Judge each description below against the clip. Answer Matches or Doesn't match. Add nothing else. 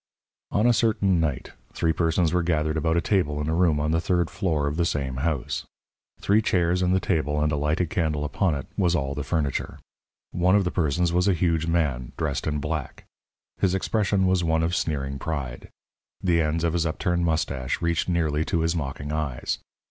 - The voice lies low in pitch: Matches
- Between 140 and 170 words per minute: Doesn't match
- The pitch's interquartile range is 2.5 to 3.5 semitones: Matches